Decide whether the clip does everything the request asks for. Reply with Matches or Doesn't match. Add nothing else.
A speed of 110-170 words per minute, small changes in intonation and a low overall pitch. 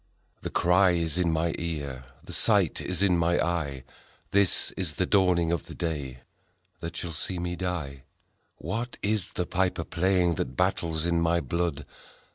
Matches